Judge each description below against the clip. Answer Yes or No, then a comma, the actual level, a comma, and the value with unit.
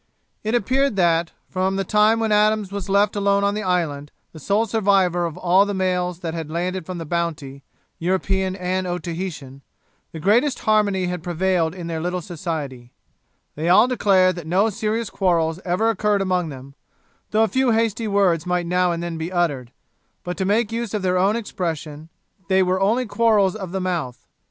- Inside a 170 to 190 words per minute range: Yes, average, 185 wpm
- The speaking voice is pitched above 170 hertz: Yes, medium, 185 Hz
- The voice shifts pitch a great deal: No, average, 3.2 semitones